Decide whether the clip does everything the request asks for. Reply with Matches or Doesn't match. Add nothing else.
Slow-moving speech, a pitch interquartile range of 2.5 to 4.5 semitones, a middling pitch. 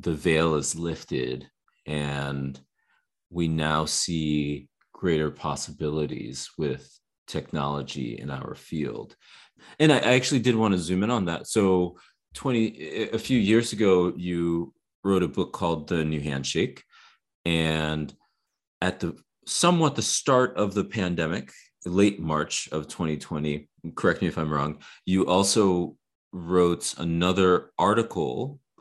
Doesn't match